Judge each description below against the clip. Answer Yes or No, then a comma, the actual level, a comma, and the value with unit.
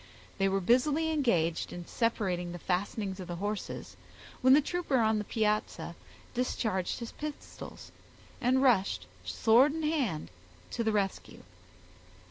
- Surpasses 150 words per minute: No, slow, 135 wpm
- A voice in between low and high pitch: No, high, 220 Hz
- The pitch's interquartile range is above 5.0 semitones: Yes, wide, 5.5 semitones